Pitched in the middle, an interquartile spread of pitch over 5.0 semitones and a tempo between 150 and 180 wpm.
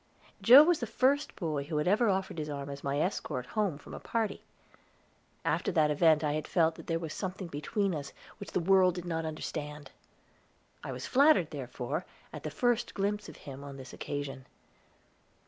No: medium, 165 Hz; wide, 5.6 semitones; average, 190 wpm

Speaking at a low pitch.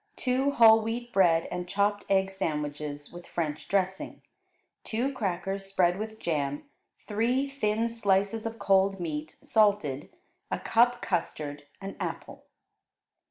No: high, 195 Hz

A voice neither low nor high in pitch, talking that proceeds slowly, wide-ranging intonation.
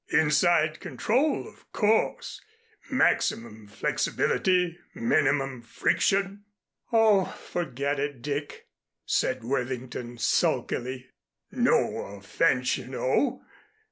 Yes: medium, 145 Hz; slow, 85 wpm; wide, 6.6 semitones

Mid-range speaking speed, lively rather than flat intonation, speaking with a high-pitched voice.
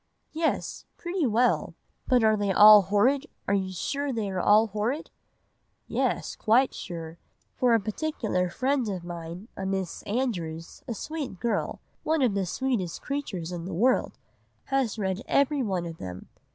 Yes: average, 150 wpm; wide, 6.0 semitones; high, 210 Hz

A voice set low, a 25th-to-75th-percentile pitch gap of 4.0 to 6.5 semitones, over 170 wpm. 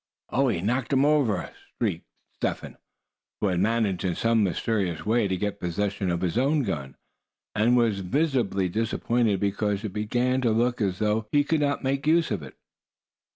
Yes: low, 110 Hz; average, 4.5 semitones; average, 180 wpm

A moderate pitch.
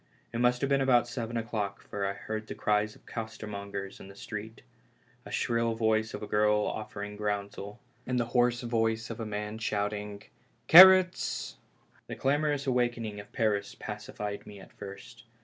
No: low, 110 Hz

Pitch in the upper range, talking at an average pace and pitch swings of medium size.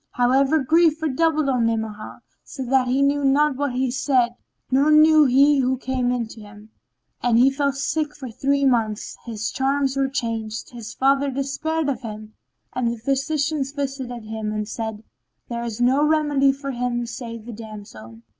Yes: very high, 260 Hz; average, 175 wpm; average, 3.4 semitones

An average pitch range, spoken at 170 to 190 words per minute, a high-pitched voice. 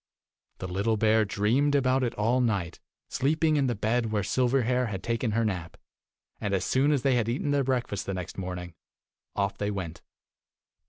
No: average, 4.4 semitones; average, 180 wpm; low, 115 Hz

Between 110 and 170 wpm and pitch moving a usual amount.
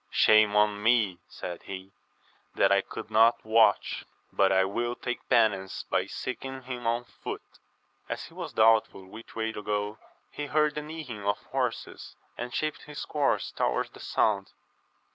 Yes: average, 160 wpm; average, 3.2 semitones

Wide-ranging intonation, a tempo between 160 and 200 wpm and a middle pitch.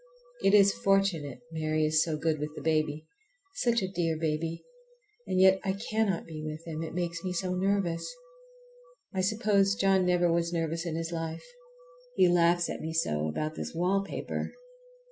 No: average, 3.1 semitones; average, 170 wpm; medium, 170 Hz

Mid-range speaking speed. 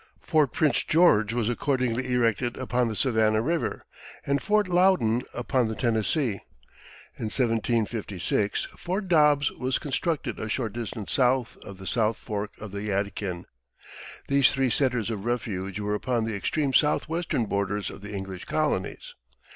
Yes: average, 145 wpm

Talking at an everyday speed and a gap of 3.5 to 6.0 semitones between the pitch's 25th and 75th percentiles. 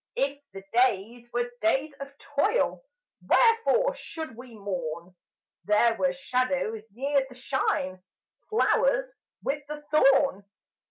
No: slow, 115 wpm; average, 4.9 semitones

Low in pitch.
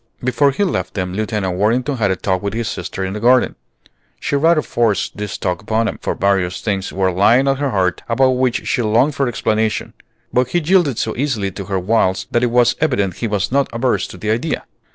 Yes: low, 115 Hz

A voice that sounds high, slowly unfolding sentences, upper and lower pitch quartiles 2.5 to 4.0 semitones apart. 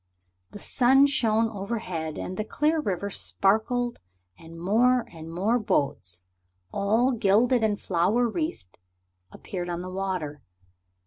No: high, 205 Hz; slow, 125 wpm; wide, 5.5 semitones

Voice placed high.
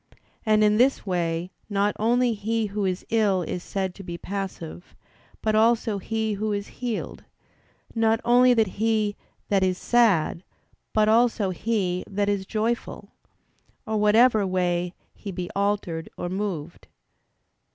Yes: high, 205 Hz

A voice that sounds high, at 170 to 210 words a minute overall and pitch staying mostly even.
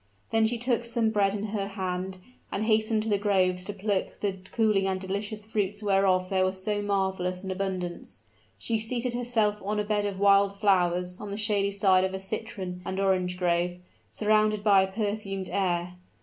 Yes: high, 200 Hz; average, 190 wpm; narrow, 2.2 semitones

